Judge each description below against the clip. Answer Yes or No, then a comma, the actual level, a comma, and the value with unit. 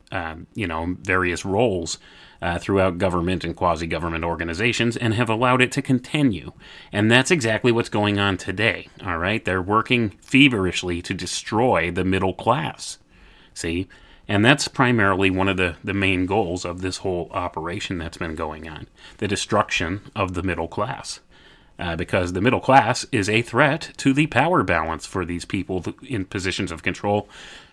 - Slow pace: No, average, 170 wpm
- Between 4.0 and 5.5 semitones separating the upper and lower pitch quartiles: Yes, average, 4.3 semitones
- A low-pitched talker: Yes, very low, 95 Hz